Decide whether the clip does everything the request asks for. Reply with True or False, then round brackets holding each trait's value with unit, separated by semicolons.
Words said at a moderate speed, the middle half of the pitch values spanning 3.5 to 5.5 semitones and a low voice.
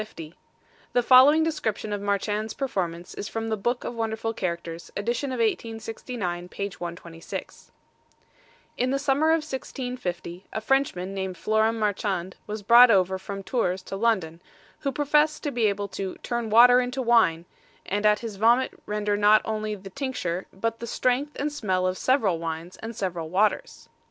False (160 wpm; 4.5 semitones; 215 Hz)